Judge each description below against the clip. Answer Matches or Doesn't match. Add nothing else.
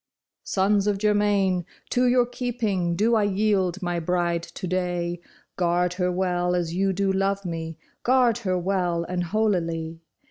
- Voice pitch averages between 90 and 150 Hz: Doesn't match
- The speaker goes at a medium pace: Matches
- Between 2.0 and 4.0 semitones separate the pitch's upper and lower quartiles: Matches